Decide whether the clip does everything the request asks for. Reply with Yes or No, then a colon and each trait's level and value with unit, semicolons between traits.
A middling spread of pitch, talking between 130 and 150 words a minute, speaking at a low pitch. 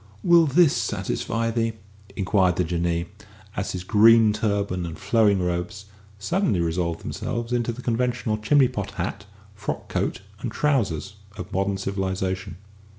Yes: average, 4.0 semitones; average, 140 wpm; low, 100 Hz